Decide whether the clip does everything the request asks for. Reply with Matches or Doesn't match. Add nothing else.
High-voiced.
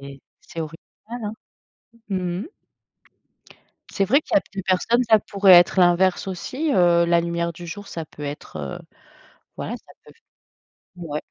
Doesn't match